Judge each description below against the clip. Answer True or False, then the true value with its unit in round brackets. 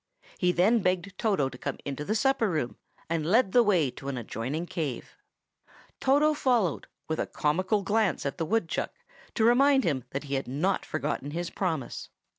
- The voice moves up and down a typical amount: False (7.1 semitones)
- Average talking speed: True (180 wpm)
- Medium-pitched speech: True (175 Hz)